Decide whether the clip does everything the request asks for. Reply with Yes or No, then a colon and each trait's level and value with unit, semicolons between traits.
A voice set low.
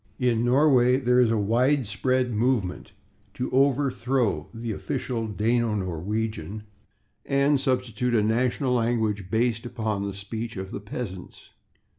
Yes: low, 115 Hz